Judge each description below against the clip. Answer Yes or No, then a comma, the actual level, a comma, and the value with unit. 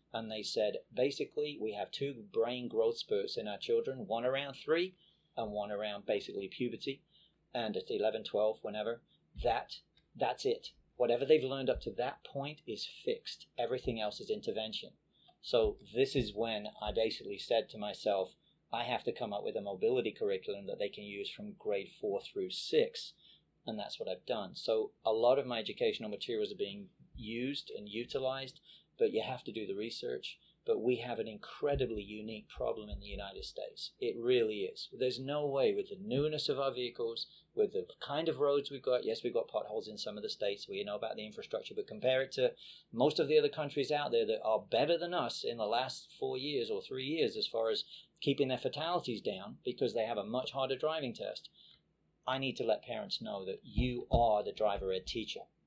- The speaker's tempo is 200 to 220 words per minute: Yes, fast, 205 wpm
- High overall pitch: Yes, very high, 370 Hz